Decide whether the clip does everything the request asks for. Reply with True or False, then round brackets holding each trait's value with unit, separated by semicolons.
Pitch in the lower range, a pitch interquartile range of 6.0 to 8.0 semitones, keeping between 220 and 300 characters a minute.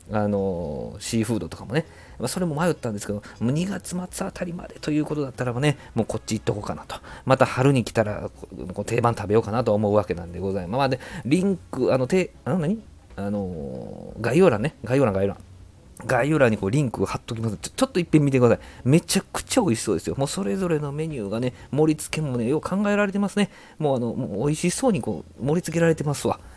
False (125 Hz; 7.4 semitones; 475 characters per minute)